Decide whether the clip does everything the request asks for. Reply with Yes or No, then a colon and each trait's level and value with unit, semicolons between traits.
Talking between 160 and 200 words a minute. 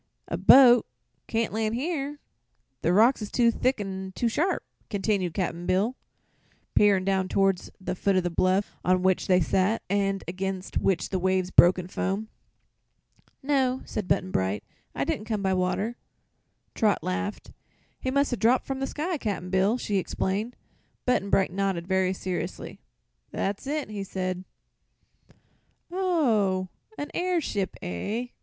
No: average, 150 wpm